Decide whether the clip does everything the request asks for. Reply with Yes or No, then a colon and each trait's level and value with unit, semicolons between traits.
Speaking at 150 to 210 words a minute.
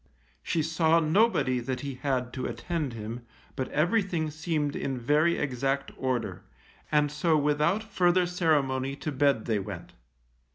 No: average, 140 wpm